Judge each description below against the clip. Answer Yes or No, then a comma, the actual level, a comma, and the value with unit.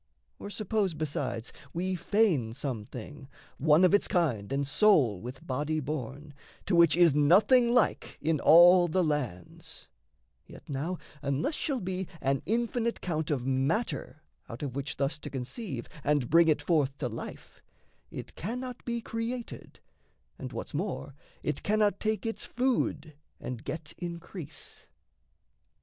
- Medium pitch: Yes, medium, 155 Hz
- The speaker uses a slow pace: No, average, 145 wpm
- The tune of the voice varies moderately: No, wide, 6.5 semitones